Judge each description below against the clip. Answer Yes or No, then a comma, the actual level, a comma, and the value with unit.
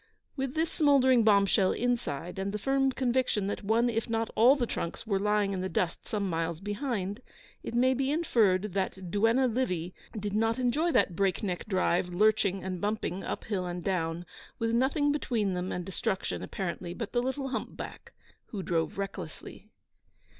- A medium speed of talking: Yes, average, 175 wpm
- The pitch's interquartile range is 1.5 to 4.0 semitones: No, average, 4.8 semitones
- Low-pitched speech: No, high, 210 Hz